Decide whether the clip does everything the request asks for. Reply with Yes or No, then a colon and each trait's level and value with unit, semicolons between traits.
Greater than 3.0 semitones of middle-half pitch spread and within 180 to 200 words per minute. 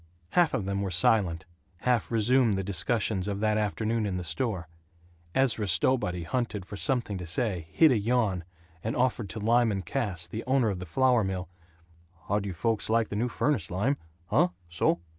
Yes: average, 4.3 semitones; average, 185 wpm